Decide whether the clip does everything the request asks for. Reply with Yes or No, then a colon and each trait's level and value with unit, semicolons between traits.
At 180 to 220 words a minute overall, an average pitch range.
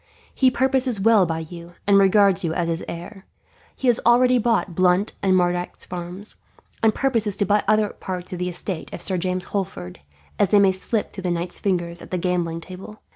Yes: average, 200 wpm; average, 3.2 semitones